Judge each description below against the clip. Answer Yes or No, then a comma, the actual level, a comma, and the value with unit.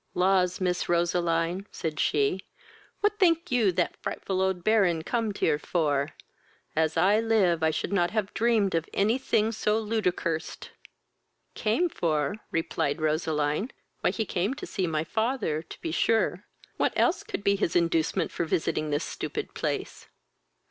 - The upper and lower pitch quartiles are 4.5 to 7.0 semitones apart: Yes, average, 5.0 semitones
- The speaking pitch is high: No, medium, 180 Hz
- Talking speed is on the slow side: No, average, 155 wpm